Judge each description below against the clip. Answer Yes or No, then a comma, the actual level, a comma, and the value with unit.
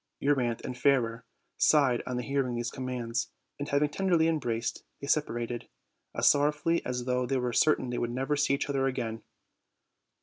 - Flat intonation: No, average, 3.0 semitones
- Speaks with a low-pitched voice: Yes, low, 130 Hz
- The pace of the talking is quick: No, average, 170 wpm